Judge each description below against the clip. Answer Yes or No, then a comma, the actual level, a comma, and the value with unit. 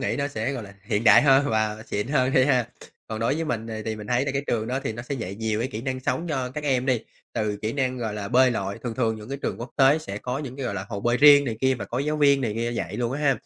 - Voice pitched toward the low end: Yes, low, 125 Hz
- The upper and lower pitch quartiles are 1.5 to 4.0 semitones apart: Yes, average, 3.6 semitones